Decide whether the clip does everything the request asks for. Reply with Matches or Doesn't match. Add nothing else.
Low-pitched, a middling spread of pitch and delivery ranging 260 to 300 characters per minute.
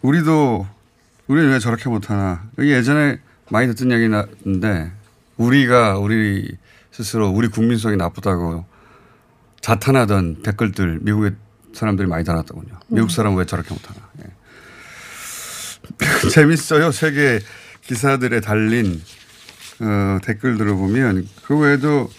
Matches